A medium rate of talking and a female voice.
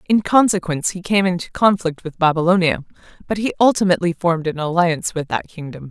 Yes: average, 175 wpm; female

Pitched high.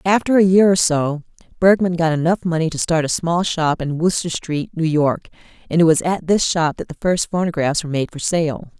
No: medium, 165 Hz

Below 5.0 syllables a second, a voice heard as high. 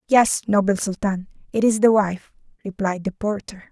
Yes: 4.7 syllables/s; high, 200 Hz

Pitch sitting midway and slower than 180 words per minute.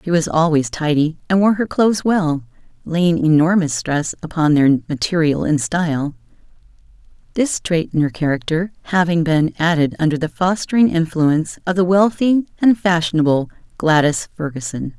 Yes: medium, 165 Hz; average, 145 wpm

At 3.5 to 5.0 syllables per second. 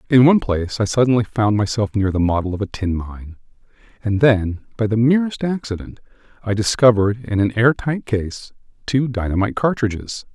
No: 5.5 syllables/s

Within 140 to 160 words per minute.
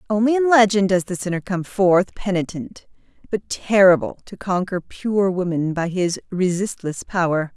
Yes: average, 150 wpm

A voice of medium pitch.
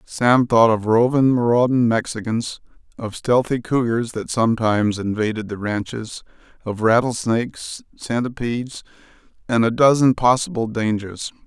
No: low, 115 Hz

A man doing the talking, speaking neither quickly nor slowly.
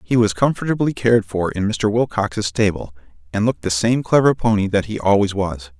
Yes: male; average, 195 wpm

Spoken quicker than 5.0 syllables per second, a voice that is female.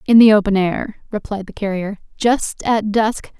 No: 4.6 syllables/s; female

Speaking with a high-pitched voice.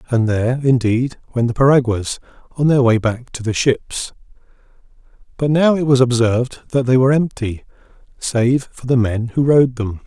No: low, 125 Hz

